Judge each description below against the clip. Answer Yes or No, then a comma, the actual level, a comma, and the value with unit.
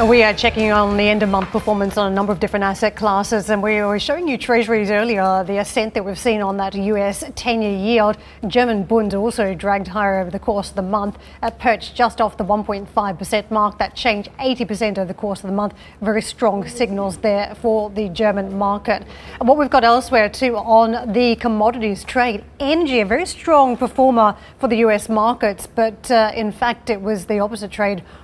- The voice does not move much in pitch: Yes, narrow, 2.3 semitones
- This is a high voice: Yes, high, 215 Hz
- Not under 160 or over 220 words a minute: Yes, average, 200 wpm